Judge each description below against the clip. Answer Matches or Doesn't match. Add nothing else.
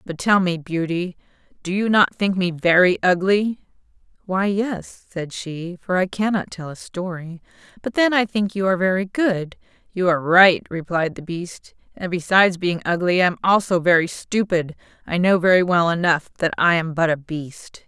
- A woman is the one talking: Matches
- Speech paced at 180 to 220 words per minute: Matches